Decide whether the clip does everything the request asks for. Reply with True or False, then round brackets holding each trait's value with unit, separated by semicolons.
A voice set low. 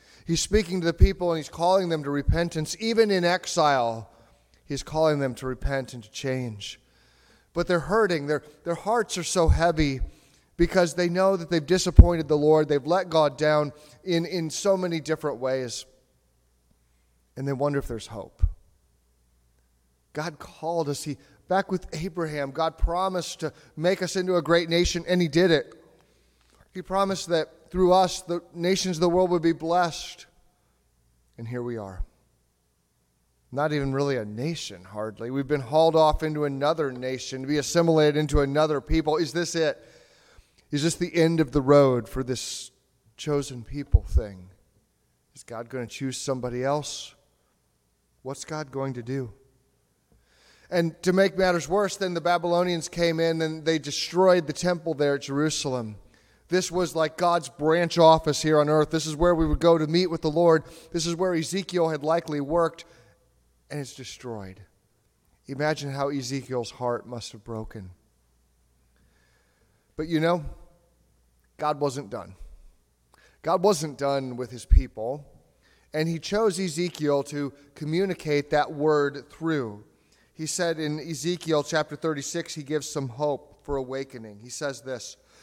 False (150 Hz)